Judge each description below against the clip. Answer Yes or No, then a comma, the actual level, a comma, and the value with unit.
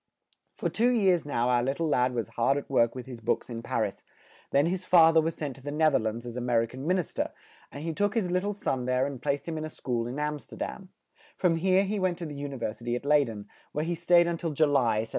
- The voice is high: No, medium, 145 Hz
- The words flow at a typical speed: No, fast, 305 wpm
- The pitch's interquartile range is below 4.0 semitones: No, wide, 5.5 semitones